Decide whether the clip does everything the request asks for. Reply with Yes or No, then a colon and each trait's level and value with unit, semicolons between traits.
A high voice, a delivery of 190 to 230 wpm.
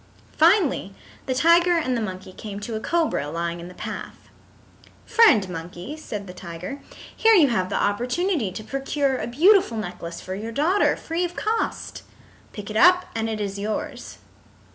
No: high, 230 Hz; average, 170 wpm